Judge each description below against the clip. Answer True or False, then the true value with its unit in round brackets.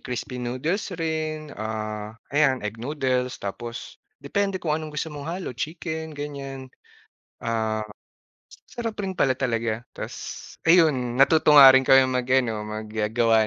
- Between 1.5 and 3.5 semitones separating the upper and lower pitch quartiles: False (5.2 semitones)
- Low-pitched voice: True (130 Hz)